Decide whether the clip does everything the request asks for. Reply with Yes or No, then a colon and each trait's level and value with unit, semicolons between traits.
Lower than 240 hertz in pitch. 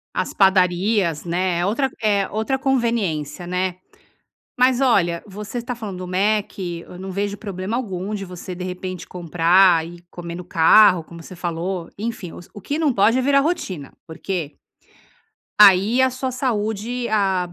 Yes: high, 190 Hz